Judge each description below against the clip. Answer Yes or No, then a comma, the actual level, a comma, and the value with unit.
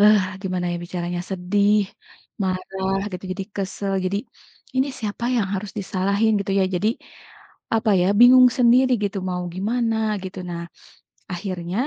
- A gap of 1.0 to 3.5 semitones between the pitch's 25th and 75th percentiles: Yes, average, 2.7 semitones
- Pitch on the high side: Yes, high, 195 Hz